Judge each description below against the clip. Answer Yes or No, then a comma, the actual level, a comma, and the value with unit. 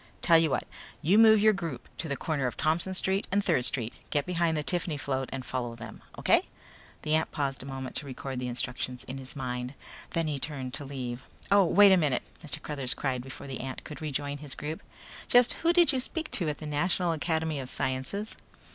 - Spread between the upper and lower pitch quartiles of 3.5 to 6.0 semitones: Yes, average, 4.6 semitones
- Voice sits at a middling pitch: Yes, medium, 145 Hz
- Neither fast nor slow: No, fast, 220 wpm